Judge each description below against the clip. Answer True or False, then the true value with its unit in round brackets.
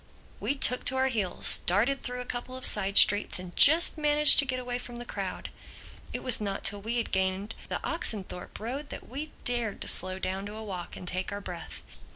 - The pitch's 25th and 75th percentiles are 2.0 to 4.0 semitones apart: False (4.8 semitones)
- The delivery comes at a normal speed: False (215 wpm)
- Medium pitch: False (225 Hz)